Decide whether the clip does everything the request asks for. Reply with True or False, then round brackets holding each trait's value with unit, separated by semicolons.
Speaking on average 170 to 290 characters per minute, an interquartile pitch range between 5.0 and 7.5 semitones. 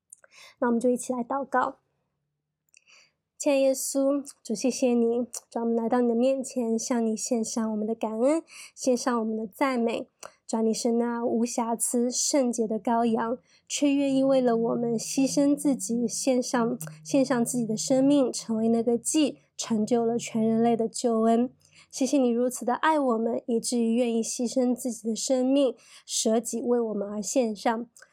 False (250 characters per minute; 2.4 semitones)